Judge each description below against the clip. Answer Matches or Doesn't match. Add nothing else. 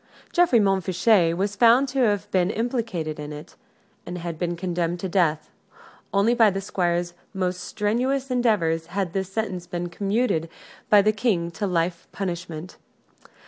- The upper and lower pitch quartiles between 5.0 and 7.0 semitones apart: Doesn't match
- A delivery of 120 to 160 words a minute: Matches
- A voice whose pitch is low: Doesn't match